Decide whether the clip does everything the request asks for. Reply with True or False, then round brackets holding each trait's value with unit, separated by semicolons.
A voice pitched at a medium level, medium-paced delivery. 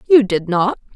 False (215 Hz; 190 wpm)